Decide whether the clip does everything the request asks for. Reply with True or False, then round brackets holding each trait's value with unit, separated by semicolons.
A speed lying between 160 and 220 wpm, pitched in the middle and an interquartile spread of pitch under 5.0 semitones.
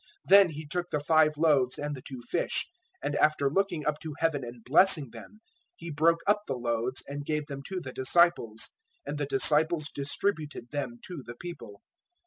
True (185 wpm; 150 Hz; 4.0 semitones)